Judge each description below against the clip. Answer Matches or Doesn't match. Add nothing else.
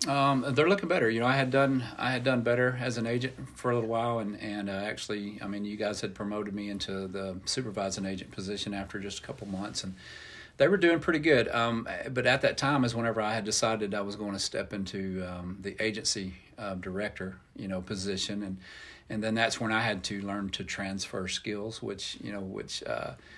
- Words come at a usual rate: Doesn't match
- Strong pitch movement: Doesn't match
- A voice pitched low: Matches